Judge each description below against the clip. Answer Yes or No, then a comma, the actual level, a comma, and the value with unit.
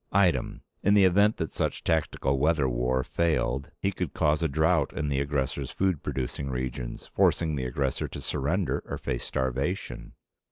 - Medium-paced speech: Yes, average, 165 wpm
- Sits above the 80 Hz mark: No, very low, 70 Hz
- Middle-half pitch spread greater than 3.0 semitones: Yes, average, 4.2 semitones